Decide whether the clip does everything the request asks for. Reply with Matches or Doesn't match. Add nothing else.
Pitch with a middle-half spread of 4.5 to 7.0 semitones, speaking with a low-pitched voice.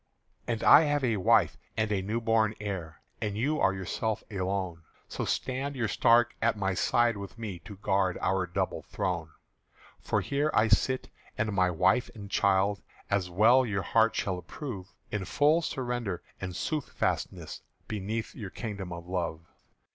Doesn't match